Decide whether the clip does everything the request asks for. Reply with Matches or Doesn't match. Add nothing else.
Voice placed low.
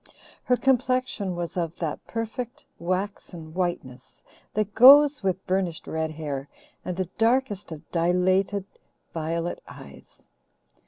Doesn't match